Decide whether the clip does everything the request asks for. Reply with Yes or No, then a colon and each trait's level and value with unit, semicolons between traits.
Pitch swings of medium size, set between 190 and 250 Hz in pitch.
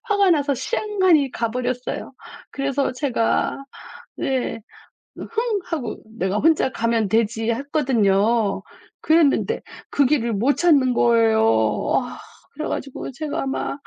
No: average, 4.8 semitones; very high, 265 Hz